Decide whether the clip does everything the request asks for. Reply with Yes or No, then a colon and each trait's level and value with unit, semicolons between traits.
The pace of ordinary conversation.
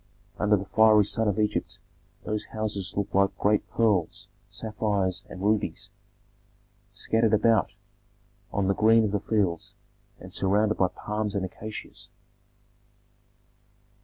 No: slow, 125 wpm